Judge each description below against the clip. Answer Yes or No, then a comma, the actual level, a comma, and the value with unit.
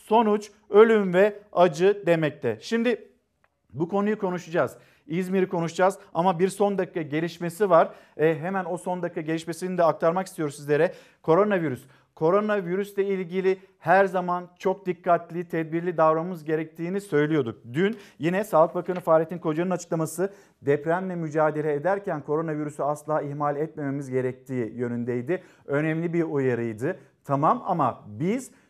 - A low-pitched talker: No, medium, 170 Hz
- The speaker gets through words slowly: No, average, 125 wpm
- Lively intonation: No, average, 3.6 semitones